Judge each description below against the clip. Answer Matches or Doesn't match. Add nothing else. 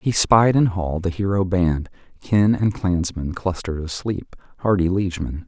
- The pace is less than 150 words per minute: Doesn't match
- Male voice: Matches